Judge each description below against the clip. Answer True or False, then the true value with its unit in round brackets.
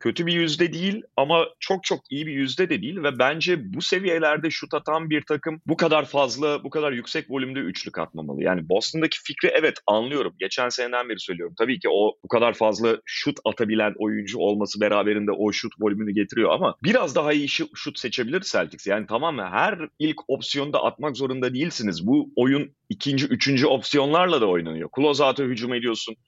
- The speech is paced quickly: True (185 wpm)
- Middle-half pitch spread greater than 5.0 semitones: True (5.5 semitones)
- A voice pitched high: False (140 Hz)